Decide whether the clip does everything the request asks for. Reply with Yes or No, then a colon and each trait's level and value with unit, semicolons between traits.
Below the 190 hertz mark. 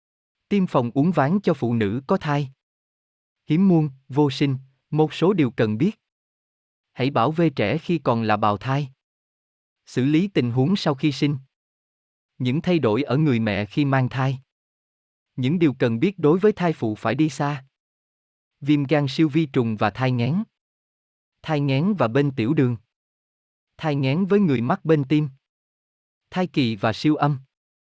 Yes: medium, 140 Hz